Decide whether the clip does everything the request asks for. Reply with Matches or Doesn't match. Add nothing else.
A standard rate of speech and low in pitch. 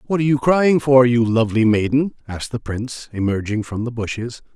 Matches